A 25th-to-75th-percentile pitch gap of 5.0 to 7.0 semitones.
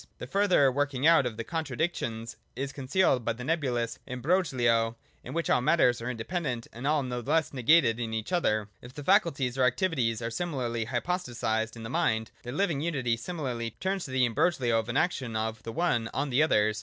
Yes: wide, 5.4 semitones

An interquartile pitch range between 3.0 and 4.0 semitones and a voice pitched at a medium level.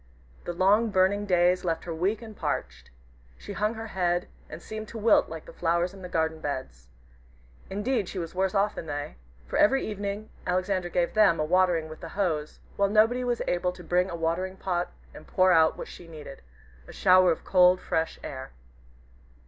Yes: average, 3.5 semitones; medium, 180 Hz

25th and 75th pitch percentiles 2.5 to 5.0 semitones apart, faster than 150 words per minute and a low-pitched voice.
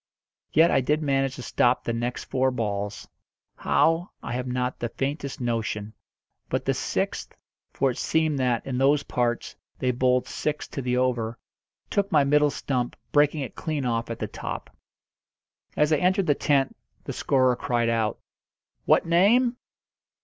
Yes: average, 3.5 semitones; average, 165 wpm; low, 130 Hz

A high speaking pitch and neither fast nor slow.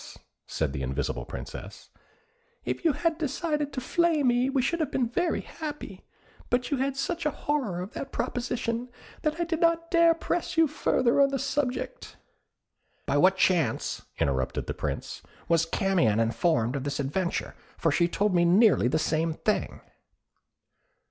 Yes: high, 245 Hz; average, 160 wpm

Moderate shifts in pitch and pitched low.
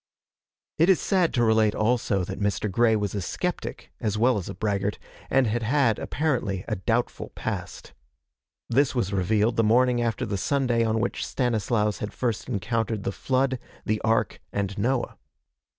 Yes: average, 3.1 semitones; low, 115 Hz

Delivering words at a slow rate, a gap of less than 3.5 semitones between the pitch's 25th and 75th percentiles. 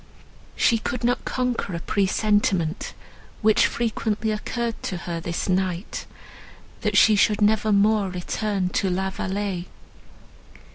Yes: slow, 115 wpm; average, 2.8 semitones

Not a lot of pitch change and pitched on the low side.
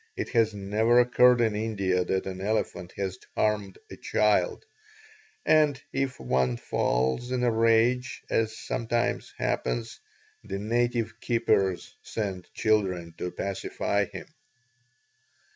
No: average, 3.9 semitones; low, 110 Hz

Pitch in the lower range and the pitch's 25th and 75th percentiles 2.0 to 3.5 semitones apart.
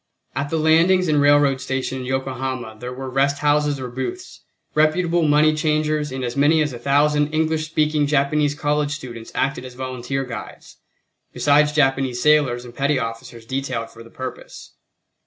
No: medium, 145 Hz; average, 2.8 semitones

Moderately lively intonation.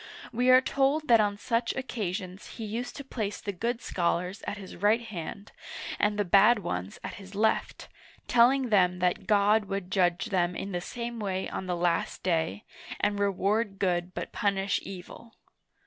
Yes: average, 3.8 semitones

